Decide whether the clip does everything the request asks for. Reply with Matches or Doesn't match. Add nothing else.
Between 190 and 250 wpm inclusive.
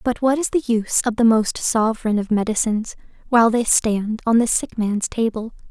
Matches